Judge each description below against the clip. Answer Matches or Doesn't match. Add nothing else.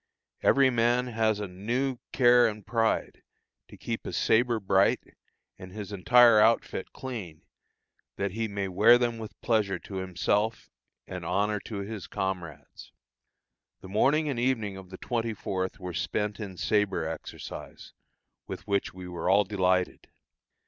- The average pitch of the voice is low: Matches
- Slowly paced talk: Doesn't match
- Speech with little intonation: Doesn't match